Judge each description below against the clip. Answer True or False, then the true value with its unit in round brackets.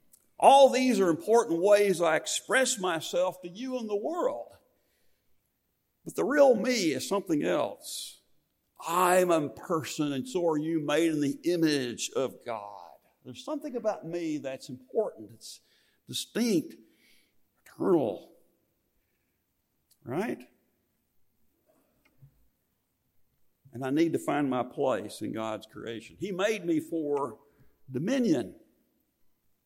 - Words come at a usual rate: False (115 wpm)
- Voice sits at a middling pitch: True (165 Hz)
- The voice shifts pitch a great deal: True (7.3 semitones)